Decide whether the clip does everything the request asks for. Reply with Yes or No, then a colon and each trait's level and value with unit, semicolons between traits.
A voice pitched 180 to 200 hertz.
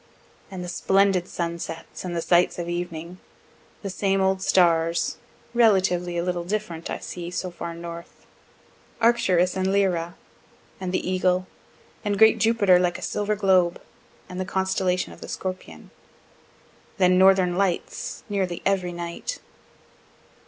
Yes: medium, 185 Hz